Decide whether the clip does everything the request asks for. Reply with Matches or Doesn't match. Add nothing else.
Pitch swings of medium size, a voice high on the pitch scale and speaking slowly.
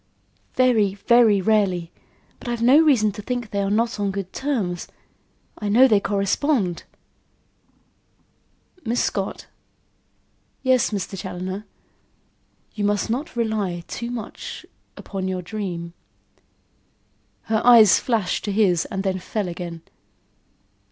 Matches